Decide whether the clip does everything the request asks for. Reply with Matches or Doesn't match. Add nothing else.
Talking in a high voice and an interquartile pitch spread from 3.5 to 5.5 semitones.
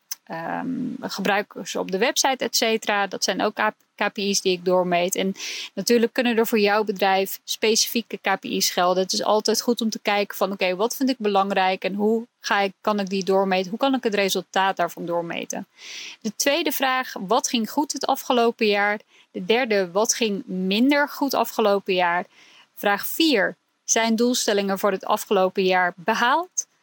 Matches